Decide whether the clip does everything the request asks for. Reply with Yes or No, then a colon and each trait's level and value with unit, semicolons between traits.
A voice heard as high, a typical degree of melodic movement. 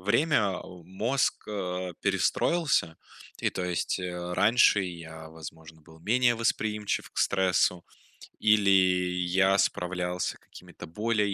No: very low, 90 Hz; average, 3.1 semitones